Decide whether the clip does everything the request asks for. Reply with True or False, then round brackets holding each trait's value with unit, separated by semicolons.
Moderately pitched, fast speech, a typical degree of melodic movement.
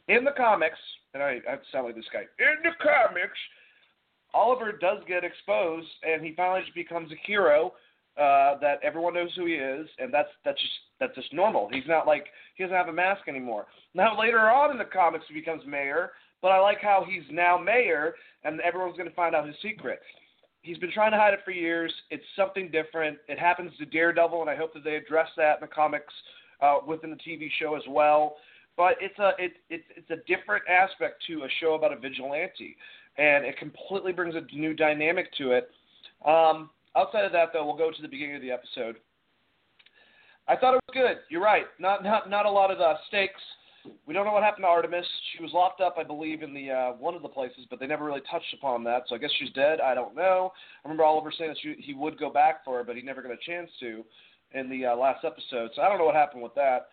True (165 Hz; 235 wpm; 4.2 semitones)